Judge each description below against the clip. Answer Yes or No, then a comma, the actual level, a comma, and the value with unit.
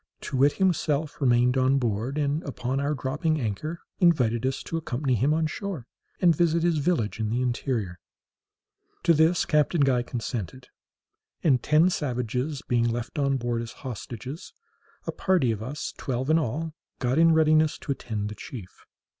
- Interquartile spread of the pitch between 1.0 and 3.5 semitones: No, average, 4.5 semitones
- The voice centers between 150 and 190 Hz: No, low, 135 Hz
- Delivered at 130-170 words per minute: Yes, average, 165 wpm